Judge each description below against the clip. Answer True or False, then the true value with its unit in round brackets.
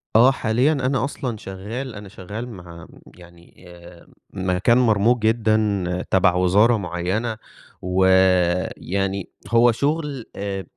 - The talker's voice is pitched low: True (100 Hz)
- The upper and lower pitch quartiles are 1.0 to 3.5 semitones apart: False (4.3 semitones)